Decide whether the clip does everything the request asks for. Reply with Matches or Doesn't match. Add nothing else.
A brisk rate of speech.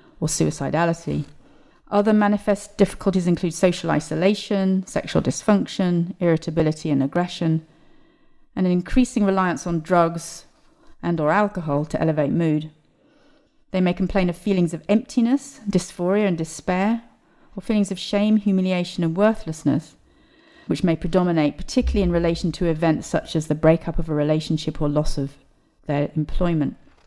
Doesn't match